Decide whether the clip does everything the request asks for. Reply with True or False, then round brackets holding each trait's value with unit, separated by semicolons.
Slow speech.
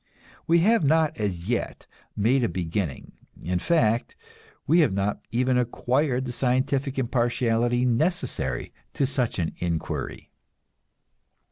True (120 wpm)